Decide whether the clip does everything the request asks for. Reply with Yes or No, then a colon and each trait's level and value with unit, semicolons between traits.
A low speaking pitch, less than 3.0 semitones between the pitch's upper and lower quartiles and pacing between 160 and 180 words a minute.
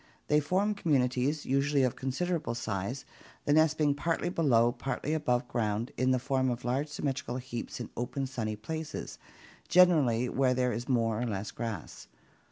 No: low, 130 Hz; average, 3.6 semitones; average, 165 wpm